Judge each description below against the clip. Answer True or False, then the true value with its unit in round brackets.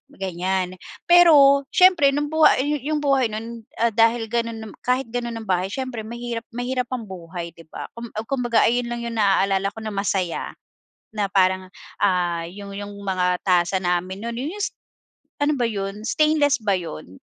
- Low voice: False (225 Hz)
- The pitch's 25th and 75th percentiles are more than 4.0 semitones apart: True (4.8 semitones)